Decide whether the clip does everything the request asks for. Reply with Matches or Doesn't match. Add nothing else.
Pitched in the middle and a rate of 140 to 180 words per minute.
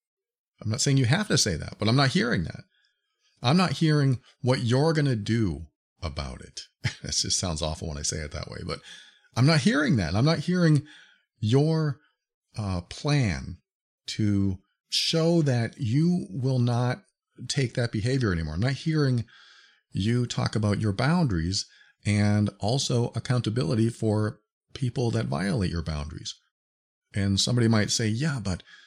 Doesn't match